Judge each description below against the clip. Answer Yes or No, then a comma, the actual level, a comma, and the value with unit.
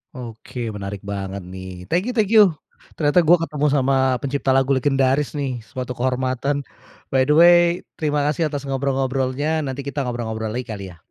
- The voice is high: No, low, 135 Hz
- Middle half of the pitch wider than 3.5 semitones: No, average, 2.8 semitones